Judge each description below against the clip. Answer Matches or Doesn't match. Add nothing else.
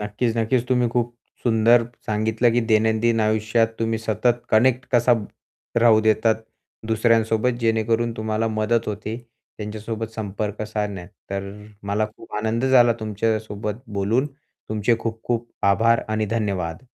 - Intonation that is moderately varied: Doesn't match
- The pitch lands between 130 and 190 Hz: Doesn't match